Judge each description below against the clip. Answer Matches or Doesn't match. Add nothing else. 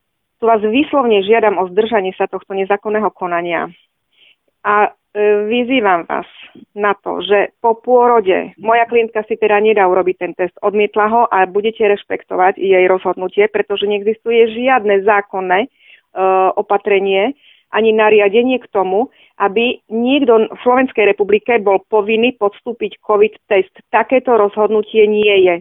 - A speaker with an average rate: Matches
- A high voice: Matches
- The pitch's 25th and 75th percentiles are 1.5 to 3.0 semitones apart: Matches